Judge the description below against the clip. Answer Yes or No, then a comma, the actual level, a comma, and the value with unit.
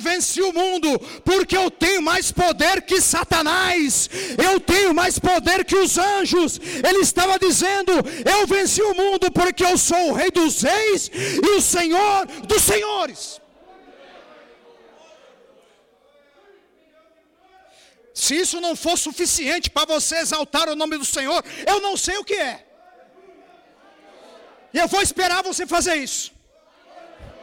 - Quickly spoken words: No, average, 135 wpm